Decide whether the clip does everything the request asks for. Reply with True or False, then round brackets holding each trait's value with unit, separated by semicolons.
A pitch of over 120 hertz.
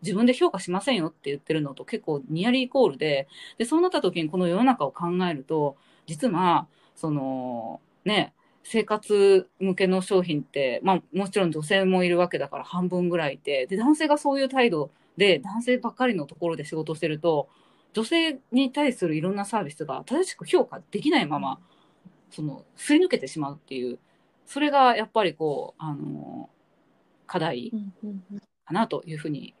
True (185 Hz)